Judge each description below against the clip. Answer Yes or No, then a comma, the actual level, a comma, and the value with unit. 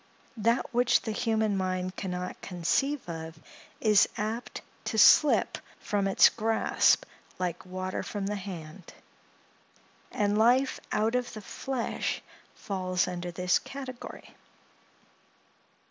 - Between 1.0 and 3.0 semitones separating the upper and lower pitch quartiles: No, average, 4.0 semitones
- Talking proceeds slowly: Yes, slow, 115 wpm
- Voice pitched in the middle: No, high, 205 Hz